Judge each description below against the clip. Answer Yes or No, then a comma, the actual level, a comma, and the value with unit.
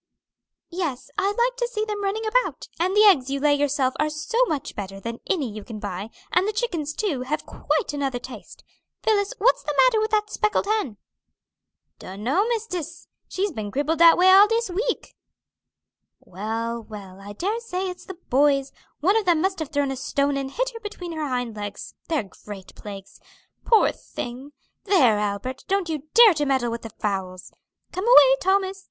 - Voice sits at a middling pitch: No, very high, 305 Hz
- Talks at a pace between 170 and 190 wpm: Yes, average, 185 wpm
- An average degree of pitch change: No, wide, 8.6 semitones